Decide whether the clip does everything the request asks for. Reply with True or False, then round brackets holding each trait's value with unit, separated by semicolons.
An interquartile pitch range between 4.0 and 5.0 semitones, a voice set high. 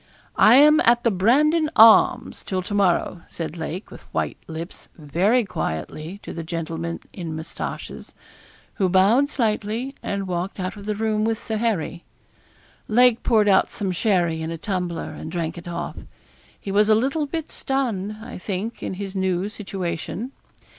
True (4.6 semitones; 195 Hz)